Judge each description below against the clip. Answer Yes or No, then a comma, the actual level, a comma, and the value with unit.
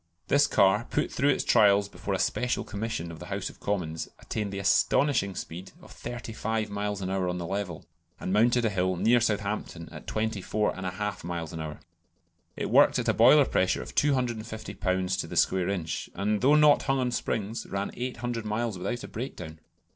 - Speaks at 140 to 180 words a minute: No, average, 190 wpm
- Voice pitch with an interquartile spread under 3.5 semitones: No, average, 4.1 semitones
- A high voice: No, low, 105 Hz